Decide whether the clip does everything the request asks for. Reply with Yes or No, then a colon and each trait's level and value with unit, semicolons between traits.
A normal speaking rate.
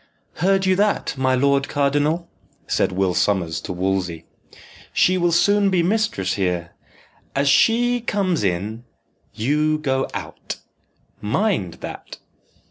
No: slow, 125 wpm